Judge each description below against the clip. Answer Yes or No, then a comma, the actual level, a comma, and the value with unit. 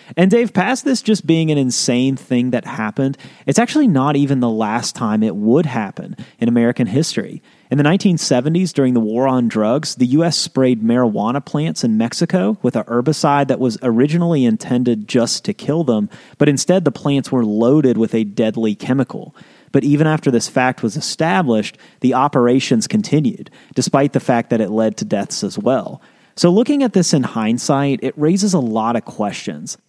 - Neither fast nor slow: Yes, average, 185 wpm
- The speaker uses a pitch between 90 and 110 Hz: No, low, 135 Hz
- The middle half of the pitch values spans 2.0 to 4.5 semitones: No, wide, 5.6 semitones